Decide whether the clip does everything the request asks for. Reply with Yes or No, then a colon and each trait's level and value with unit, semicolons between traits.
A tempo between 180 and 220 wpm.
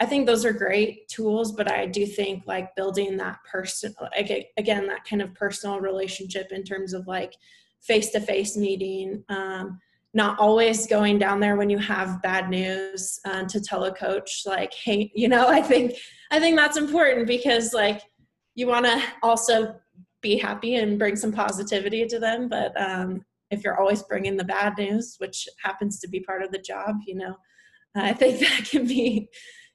Yes: average, 185 wpm